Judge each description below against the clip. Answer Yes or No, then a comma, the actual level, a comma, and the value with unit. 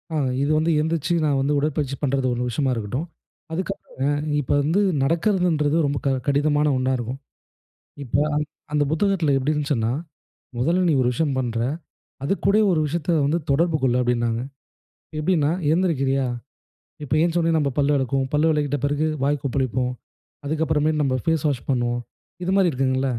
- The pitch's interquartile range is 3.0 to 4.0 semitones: Yes, average, 3.3 semitones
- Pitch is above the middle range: No, medium, 145 Hz